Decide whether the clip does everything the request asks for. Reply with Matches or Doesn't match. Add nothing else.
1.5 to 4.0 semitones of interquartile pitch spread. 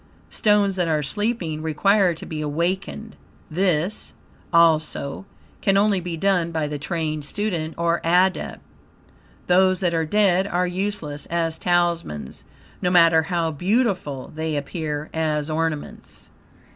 Matches